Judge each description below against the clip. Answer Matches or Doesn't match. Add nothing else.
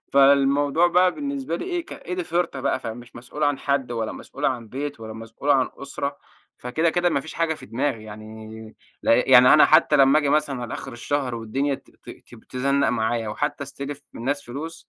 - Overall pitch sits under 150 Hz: Matches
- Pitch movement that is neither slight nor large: Matches